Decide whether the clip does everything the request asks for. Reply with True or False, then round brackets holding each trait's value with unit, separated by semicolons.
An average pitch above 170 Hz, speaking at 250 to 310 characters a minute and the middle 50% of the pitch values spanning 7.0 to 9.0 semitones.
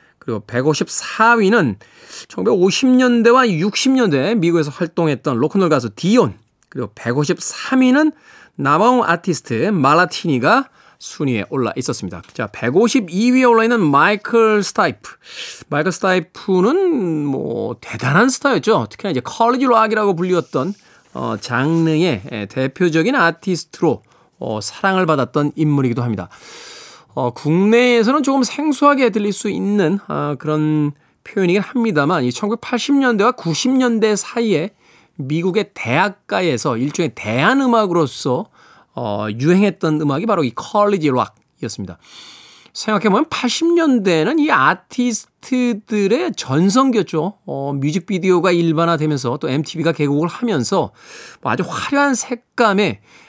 True (185 Hz; 285 characters per minute; 7.5 semitones)